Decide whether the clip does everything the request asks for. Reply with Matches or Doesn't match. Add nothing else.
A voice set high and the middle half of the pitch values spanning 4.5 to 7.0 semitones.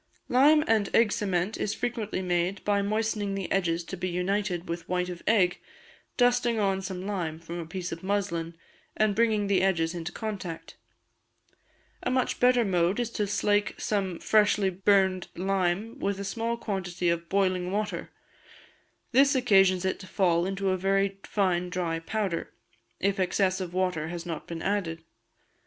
Doesn't match